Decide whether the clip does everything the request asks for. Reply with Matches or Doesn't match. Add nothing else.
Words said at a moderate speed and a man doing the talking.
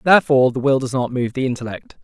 Doesn't match